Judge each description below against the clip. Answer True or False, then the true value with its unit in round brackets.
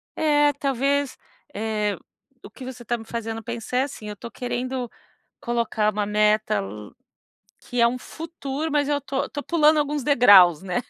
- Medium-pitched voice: False (245 Hz)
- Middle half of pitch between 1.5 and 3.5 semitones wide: False (4.5 semitones)